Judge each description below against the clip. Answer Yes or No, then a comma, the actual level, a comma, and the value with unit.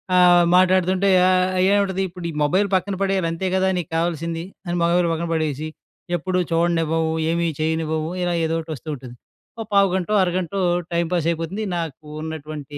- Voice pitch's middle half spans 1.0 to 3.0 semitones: Yes, narrow, 2.5 semitones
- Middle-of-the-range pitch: Yes, medium, 170 Hz